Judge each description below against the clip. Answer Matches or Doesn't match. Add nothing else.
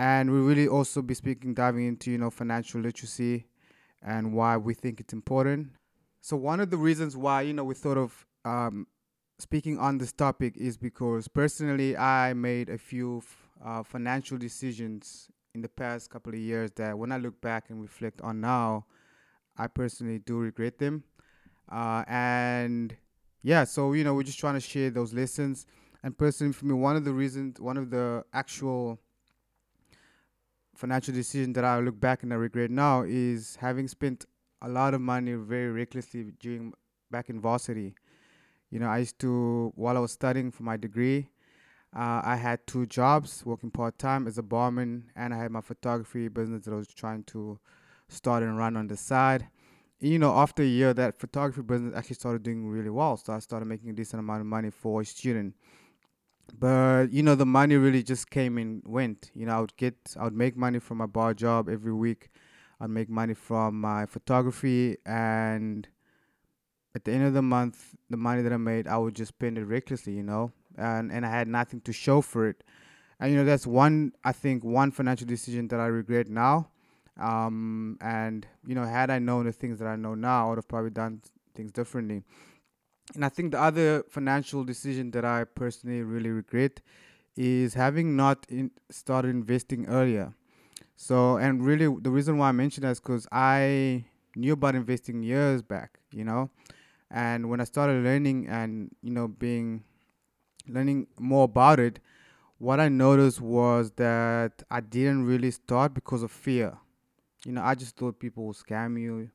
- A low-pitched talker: Matches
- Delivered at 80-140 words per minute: Doesn't match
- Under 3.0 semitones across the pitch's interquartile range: Matches